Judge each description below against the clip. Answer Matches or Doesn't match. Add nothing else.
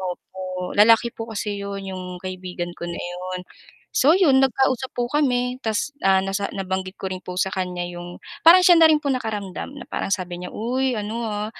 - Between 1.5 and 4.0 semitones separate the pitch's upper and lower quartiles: Doesn't match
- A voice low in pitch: Doesn't match